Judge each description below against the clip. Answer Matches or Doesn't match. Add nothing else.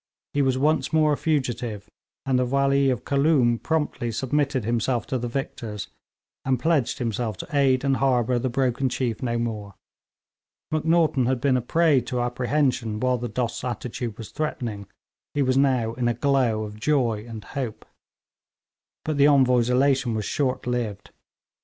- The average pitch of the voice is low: Matches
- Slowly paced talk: Doesn't match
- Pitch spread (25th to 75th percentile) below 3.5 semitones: Matches